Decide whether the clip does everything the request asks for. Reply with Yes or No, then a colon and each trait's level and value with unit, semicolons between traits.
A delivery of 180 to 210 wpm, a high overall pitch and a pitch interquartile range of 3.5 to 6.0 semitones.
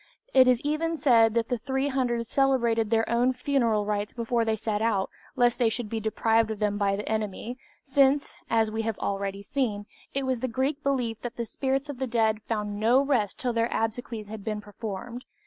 No: average, 200 wpm; high, 230 Hz; average, 3.1 semitones